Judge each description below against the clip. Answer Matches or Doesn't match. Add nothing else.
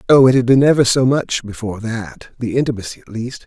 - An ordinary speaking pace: Doesn't match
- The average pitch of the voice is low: Matches